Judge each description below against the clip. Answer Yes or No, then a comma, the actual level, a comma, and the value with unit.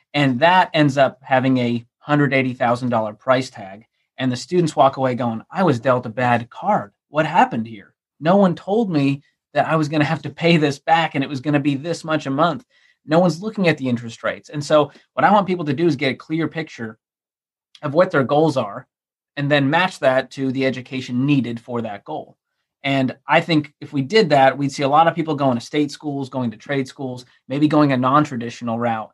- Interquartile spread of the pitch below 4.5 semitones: Yes, average, 3.4 semitones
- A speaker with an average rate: No, fast, 230 wpm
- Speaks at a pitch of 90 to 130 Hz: No, medium, 140 Hz